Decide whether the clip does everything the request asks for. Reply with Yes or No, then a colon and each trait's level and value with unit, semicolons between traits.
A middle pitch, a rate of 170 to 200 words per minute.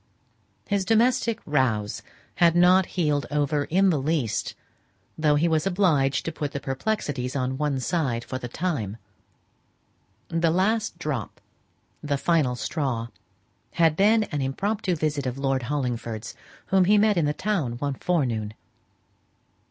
No: medium, 150 Hz; average, 145 wpm